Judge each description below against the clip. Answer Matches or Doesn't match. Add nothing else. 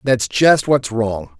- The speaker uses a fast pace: Doesn't match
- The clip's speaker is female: Doesn't match